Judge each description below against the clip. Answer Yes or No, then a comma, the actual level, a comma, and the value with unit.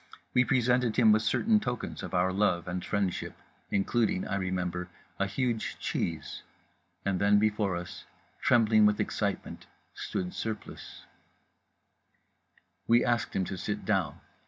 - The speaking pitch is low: Yes, low, 105 Hz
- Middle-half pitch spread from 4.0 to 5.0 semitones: No, average, 3.6 semitones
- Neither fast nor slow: No, slow, 125 wpm